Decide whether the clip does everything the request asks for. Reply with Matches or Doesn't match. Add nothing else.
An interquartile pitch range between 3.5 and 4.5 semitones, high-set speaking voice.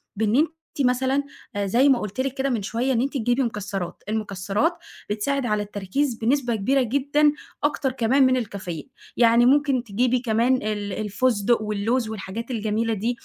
Matches